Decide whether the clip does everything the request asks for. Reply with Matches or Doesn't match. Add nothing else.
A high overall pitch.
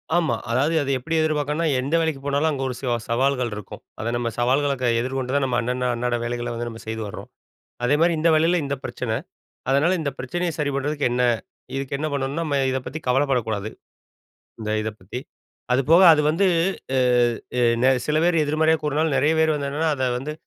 Doesn't match